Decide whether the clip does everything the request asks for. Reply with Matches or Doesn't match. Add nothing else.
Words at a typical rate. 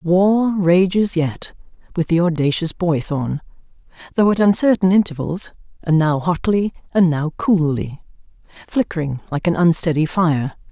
Doesn't match